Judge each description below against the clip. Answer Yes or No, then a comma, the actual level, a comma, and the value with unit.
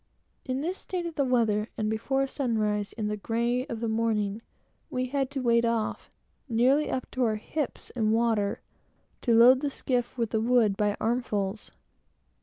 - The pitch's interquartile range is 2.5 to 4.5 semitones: Yes, average, 3.0 semitones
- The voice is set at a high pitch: Yes, high, 235 Hz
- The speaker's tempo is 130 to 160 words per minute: No, average, 175 wpm